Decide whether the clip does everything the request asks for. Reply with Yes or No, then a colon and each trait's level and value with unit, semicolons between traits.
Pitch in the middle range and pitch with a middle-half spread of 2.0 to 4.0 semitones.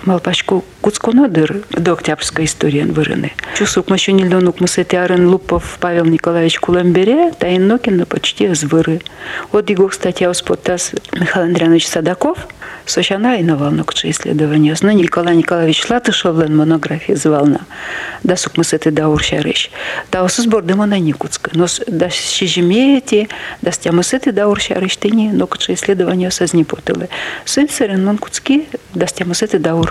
Yes: medium, 180 Hz; average, 3.7 semitones